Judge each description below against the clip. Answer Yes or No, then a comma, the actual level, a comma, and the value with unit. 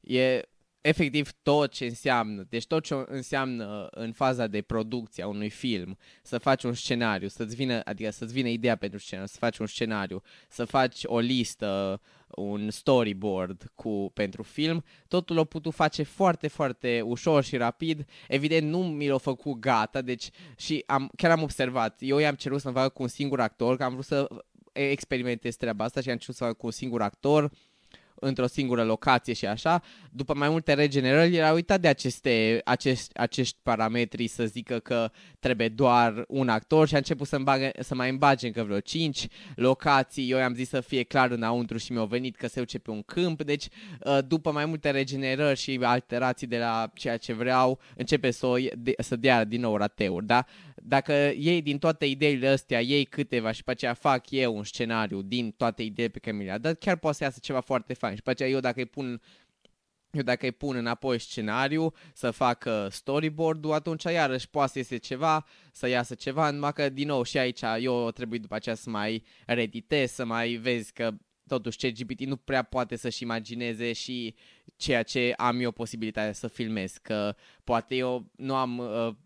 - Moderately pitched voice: No, low, 125 Hz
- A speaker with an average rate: No, fast, 195 wpm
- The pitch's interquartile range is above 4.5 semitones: No, average, 3.3 semitones